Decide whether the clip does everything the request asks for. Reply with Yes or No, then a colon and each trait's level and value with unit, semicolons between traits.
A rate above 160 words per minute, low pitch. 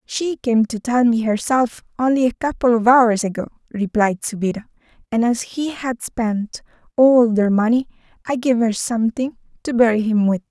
No: average, 170 wpm; high, 235 Hz